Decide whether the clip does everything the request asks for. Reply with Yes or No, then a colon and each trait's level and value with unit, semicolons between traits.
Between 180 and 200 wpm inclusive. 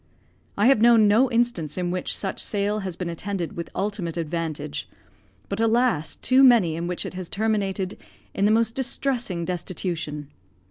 No: average, 160 wpm